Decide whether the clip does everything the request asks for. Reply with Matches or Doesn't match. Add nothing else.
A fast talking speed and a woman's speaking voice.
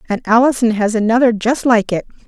Doesn't match